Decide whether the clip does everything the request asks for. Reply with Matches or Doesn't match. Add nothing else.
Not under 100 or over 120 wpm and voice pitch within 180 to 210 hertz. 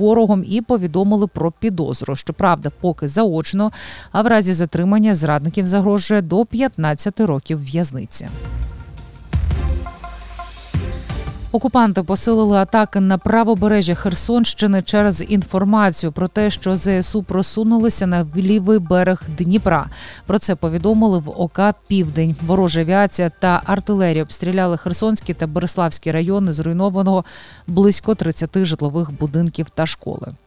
Matches